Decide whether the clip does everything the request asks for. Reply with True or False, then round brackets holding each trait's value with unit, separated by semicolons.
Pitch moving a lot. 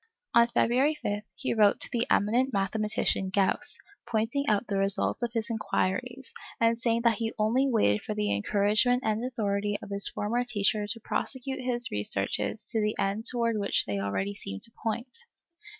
False (3.1 semitones)